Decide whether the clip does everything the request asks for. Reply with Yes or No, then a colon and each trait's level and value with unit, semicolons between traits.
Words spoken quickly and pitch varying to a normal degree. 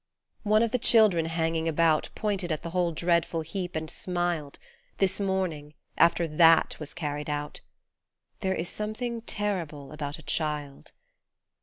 No: average, 145 wpm; average, 3.7 semitones